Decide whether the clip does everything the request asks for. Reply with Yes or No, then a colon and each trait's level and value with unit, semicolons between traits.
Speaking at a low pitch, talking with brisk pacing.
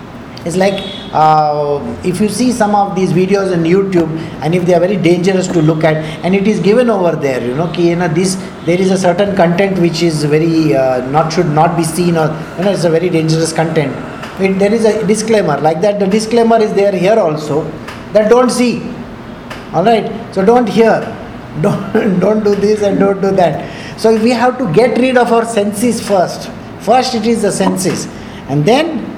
No: high, 190 Hz; fast, 210 wpm